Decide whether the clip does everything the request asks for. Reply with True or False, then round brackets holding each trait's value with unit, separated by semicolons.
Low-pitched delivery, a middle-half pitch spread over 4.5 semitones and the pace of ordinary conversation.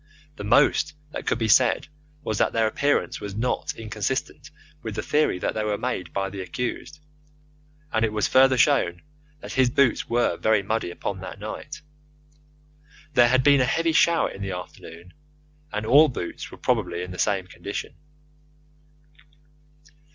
True (110 Hz; 4.9 semitones; 165 wpm)